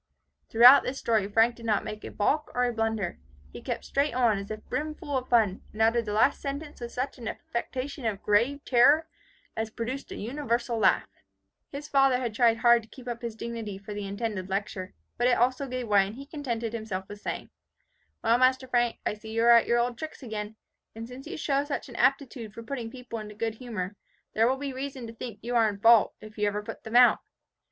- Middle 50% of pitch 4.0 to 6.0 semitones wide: No, average, 2.9 semitones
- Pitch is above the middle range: Yes, high, 235 Hz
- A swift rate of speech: Yes, fast, 225 wpm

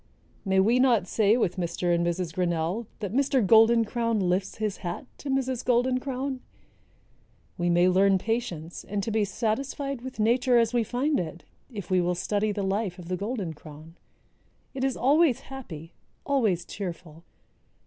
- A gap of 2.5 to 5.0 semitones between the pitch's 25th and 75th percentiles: No, wide, 5.6 semitones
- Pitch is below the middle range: No, high, 210 Hz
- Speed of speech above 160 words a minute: Yes, average, 170 wpm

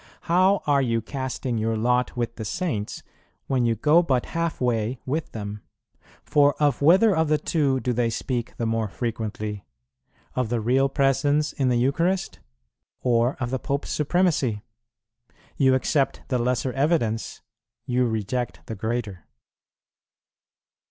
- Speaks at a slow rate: No, average, 145 wpm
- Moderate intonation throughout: Yes, average, 3.9 semitones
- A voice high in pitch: No, low, 125 Hz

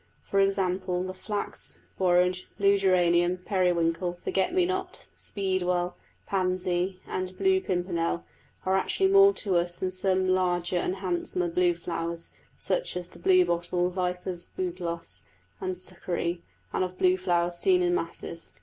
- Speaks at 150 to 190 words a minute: No, average, 140 wpm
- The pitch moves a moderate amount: No, narrow, 1.4 semitones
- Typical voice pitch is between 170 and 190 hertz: Yes, medium, 185 Hz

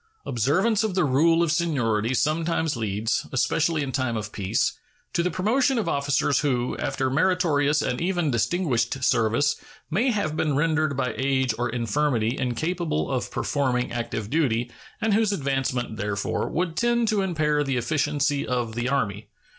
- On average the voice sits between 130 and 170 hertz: Yes, medium, 140 Hz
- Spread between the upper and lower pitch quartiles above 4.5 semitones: Yes, wide, 5.4 semitones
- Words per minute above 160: No, average, 155 wpm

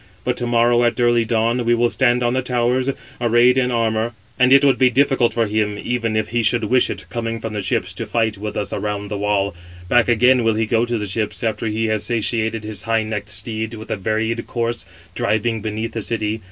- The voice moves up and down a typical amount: No, narrow, 1.8 semitones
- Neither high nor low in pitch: No, low, 115 Hz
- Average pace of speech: No, fast, 230 wpm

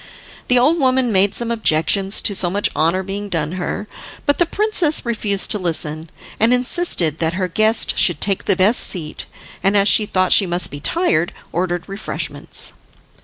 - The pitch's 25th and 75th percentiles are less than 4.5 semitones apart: No, average, 5.0 semitones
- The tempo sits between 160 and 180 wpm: Yes, average, 175 wpm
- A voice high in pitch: Yes, high, 195 Hz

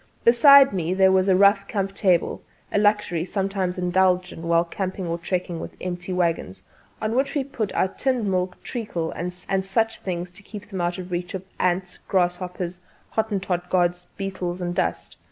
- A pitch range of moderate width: No, narrow, 2.0 semitones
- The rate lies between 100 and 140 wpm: No, average, 180 wpm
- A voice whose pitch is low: No, medium, 185 Hz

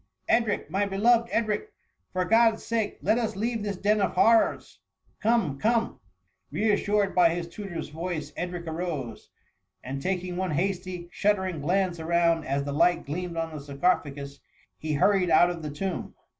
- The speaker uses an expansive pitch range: No, average, 4.1 semitones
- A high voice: No, medium, 180 Hz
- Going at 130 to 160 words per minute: No, average, 175 wpm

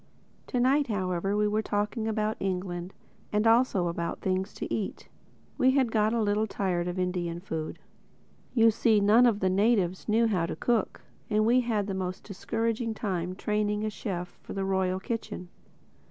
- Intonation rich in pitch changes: No, average, 3.3 semitones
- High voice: Yes, high, 205 Hz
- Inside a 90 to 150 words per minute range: No, average, 170 wpm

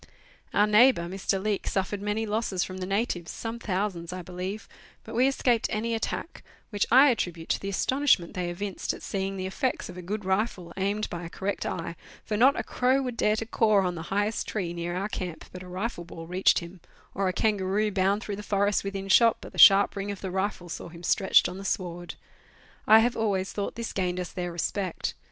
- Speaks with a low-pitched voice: No, high, 195 Hz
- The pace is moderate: No, fast, 220 wpm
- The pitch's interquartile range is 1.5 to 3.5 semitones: Yes, average, 2.8 semitones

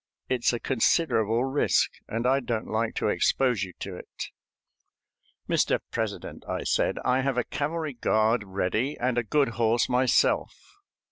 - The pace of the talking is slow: No, average, 150 wpm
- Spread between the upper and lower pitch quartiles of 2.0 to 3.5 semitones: Yes, average, 3.1 semitones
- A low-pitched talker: Yes, low, 120 Hz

